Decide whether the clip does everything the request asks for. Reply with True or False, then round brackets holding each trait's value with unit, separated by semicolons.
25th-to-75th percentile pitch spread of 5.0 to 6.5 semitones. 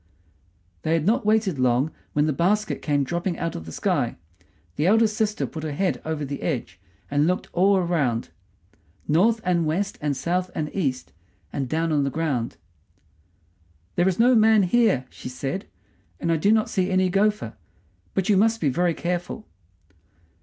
True (5.4 semitones)